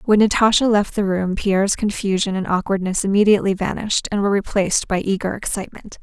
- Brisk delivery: No, average, 170 wpm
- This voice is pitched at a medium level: No, high, 200 Hz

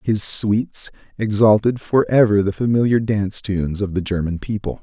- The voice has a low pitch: Yes, low, 105 Hz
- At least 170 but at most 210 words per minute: No, average, 150 wpm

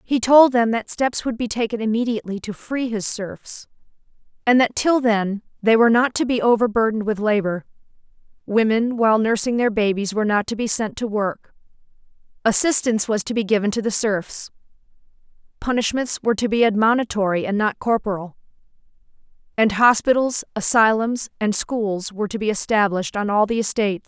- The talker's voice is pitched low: No, high, 220 Hz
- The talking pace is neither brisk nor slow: Yes, average, 160 wpm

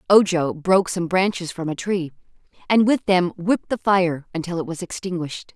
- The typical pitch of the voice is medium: Yes, medium, 180 Hz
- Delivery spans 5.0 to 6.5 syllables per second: Yes, 5.3 syllables/s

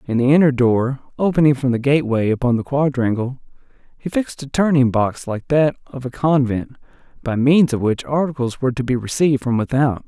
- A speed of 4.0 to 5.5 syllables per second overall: No, 5.7 syllables/s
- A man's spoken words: Yes, male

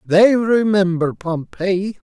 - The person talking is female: No, male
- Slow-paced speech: Yes, slow, 85 wpm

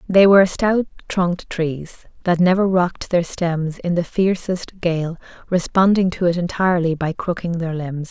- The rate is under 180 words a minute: Yes, average, 165 wpm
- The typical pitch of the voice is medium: Yes, medium, 175 Hz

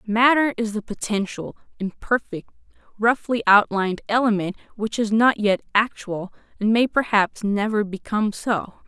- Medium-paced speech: No, slow, 130 wpm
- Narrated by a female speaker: Yes, female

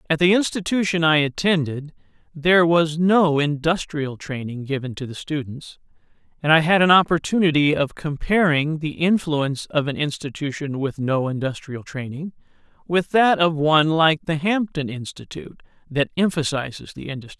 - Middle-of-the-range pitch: Yes, medium, 155 Hz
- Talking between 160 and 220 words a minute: No, average, 145 wpm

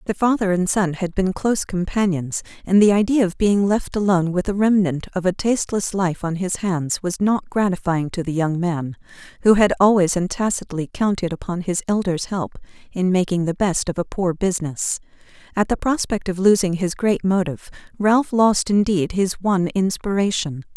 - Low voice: No, high, 190 Hz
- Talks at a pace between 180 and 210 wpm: Yes, average, 185 wpm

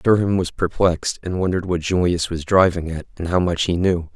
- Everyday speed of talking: No, fast, 215 wpm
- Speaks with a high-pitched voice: No, very low, 90 Hz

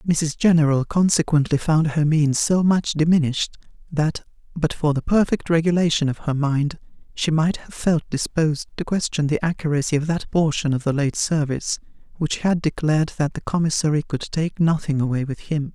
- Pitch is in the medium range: Yes, medium, 155 Hz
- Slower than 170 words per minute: No, average, 175 wpm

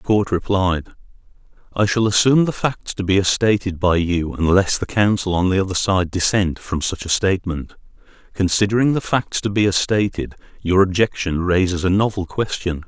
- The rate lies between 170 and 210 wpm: Yes, average, 180 wpm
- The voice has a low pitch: Yes, very low, 95 Hz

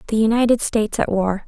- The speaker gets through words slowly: No, fast, 205 wpm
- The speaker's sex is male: No, female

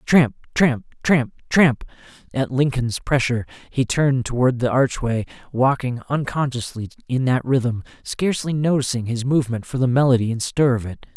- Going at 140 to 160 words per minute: Yes, average, 150 wpm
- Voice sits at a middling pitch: No, low, 130 Hz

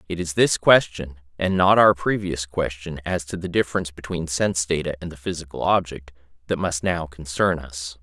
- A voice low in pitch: Yes, very low, 85 Hz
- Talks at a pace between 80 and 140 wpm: No, average, 185 wpm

